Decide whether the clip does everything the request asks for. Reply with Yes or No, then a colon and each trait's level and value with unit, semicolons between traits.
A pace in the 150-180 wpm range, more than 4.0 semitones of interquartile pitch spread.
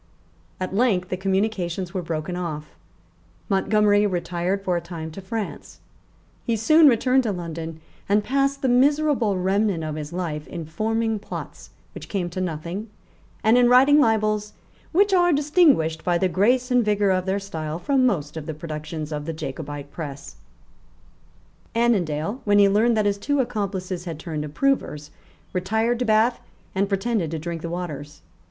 Yes: average, 165 wpm; wide, 5.4 semitones